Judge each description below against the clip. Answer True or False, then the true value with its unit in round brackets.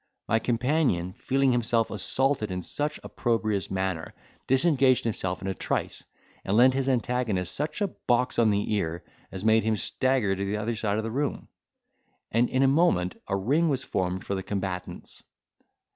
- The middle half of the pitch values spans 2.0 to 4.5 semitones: False (5.3 semitones)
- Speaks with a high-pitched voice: False (110 Hz)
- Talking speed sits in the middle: True (175 wpm)